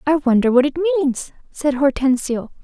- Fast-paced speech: No, average, 160 wpm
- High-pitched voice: Yes, very high, 280 Hz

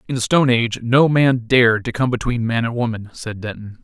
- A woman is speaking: No, male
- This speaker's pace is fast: Yes, fast, 235 wpm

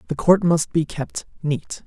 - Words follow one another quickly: No, average, 195 wpm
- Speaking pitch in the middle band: Yes, medium, 160 Hz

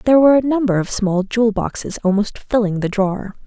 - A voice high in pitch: Yes, high, 215 Hz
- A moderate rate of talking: No, fast, 210 wpm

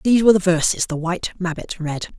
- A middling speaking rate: No, fast, 220 wpm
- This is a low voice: No, medium, 180 Hz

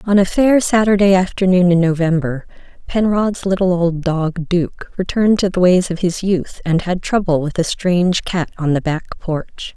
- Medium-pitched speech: Yes, medium, 180 Hz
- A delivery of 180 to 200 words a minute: Yes, average, 185 wpm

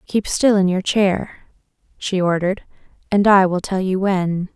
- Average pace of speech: Yes, average, 170 wpm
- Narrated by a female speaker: Yes, female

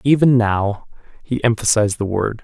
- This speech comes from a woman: No, male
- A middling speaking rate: Yes, average, 150 wpm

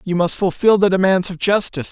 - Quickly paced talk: Yes, fast, 220 wpm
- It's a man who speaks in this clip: Yes, male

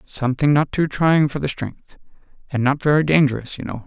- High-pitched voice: No, medium, 140 Hz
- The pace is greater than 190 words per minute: Yes, average, 200 wpm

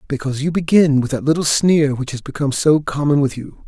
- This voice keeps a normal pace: No, fast, 230 wpm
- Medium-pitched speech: Yes, medium, 145 Hz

